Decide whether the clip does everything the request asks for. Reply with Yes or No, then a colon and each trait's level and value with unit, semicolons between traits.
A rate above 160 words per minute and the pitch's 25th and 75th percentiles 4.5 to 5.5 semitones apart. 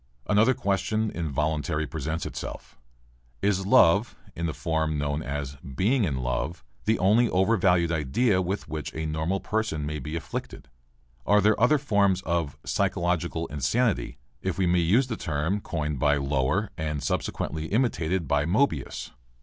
No: average, 150 wpm; average, 5.1 semitones